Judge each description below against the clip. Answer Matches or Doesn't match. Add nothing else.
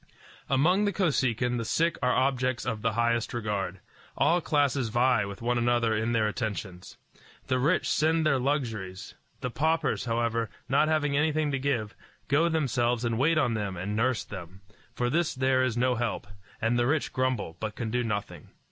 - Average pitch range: Matches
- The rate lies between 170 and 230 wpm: Matches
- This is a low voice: Matches